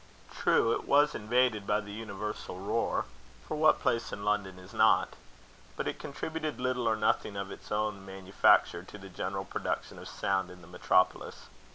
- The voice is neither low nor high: No, low, 105 Hz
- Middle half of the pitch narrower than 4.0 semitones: Yes, average, 3.3 semitones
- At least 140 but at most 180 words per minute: Yes, average, 175 wpm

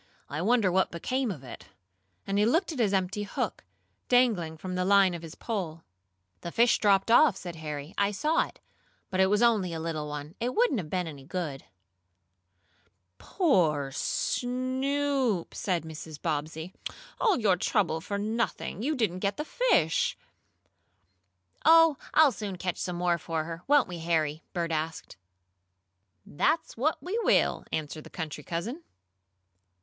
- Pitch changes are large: Yes, wide, 6.9 semitones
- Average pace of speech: Yes, average, 155 wpm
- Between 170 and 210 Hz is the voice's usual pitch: Yes, medium, 185 Hz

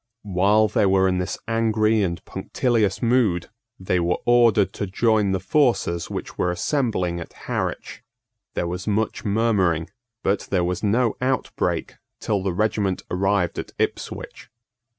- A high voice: No, low, 100 Hz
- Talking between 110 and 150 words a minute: Yes, average, 145 wpm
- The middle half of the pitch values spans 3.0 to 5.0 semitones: Yes, average, 3.5 semitones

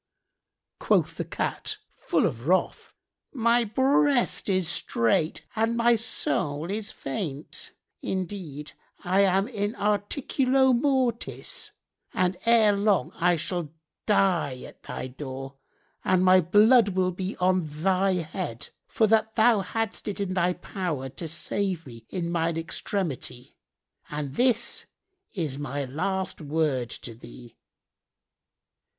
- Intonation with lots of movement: Yes, wide, 5.8 semitones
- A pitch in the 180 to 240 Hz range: Yes, medium, 185 Hz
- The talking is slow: Yes, slow, 125 wpm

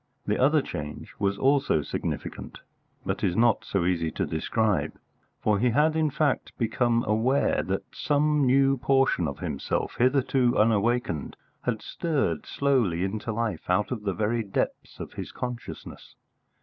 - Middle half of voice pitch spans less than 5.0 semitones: No, average, 5.3 semitones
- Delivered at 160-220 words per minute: No, average, 150 wpm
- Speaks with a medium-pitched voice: No, low, 115 Hz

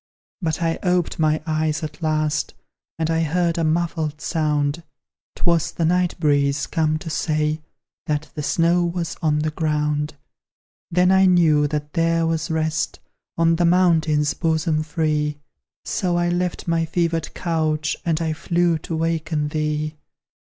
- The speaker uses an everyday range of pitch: No, narrow, 1.7 semitones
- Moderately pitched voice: Yes, medium, 160 Hz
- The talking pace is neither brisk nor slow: Yes, average, 150 wpm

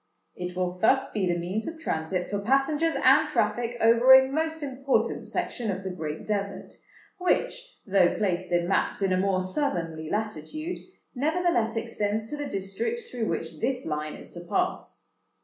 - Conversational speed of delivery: Yes, average, 165 wpm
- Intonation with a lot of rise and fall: Yes, wide, 6.9 semitones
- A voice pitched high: Yes, high, 215 Hz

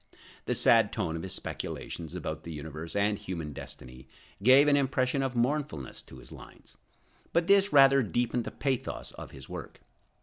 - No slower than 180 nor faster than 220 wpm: No, average, 170 wpm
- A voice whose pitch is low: Yes, low, 120 Hz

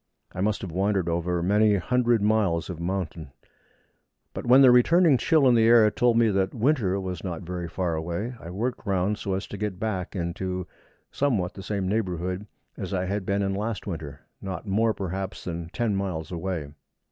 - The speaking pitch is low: Yes, very low, 95 Hz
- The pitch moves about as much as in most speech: Yes, average, 3.5 semitones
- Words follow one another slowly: No, average, 190 wpm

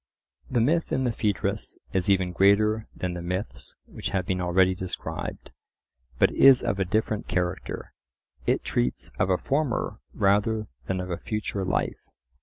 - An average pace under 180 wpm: Yes, average, 160 wpm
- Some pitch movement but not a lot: Yes, average, 3.1 semitones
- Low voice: Yes, very low, 95 Hz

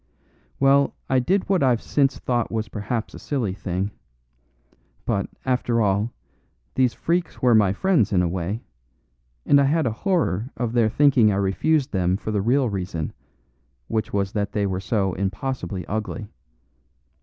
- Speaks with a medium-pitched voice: No, low, 110 Hz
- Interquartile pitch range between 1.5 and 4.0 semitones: No, average, 5.1 semitones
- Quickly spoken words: No, average, 160 wpm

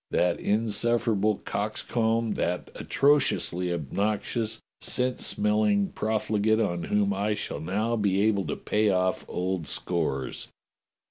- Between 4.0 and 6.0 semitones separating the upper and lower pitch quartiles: No, average, 3.1 semitones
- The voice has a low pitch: Yes, low, 105 Hz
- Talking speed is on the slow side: Yes, slow, 125 wpm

